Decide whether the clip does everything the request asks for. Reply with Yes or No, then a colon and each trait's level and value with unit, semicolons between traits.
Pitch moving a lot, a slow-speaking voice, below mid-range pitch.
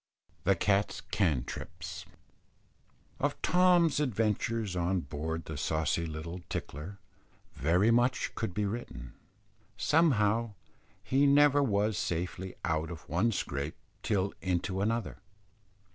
Yes: wide, 5.7 semitones; slow, 110 wpm; low, 100 Hz